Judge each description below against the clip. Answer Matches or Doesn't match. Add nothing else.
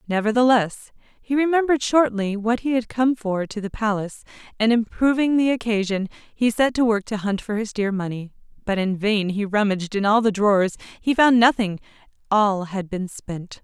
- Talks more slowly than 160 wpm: Doesn't match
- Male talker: Doesn't match